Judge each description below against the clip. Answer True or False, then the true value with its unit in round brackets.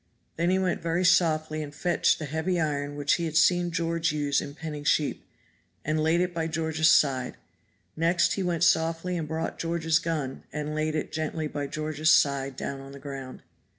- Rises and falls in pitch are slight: True (2.2 semitones)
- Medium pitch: True (155 Hz)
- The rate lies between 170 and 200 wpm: True (190 wpm)